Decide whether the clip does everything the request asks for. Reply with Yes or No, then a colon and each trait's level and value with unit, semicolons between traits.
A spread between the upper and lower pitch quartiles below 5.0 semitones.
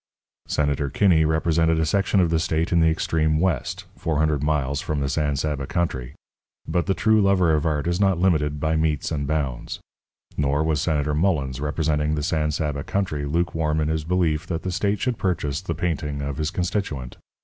Yes: narrow, 2.6 semitones